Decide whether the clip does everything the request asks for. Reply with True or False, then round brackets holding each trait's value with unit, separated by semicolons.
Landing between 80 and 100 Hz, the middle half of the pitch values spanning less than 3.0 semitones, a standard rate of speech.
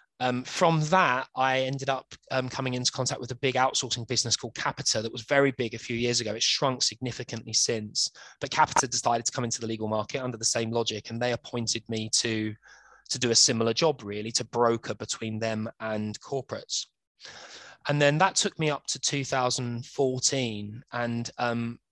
False (120 Hz; 2.5 semitones; 190 wpm)